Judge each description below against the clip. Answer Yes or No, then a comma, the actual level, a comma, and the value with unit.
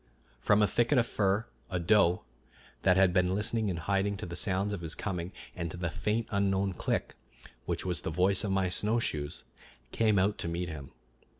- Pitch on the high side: No, very low, 95 Hz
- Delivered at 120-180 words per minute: No, average, 195 wpm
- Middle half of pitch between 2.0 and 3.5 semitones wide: Yes, average, 2.8 semitones